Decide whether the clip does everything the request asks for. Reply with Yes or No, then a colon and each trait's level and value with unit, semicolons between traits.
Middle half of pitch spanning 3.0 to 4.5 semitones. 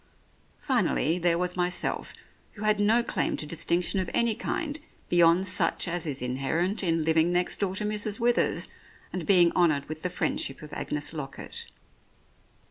Yes: average, 3.9 semitones